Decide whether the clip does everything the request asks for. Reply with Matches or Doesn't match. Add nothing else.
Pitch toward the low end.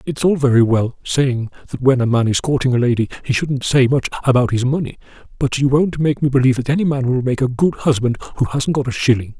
Matches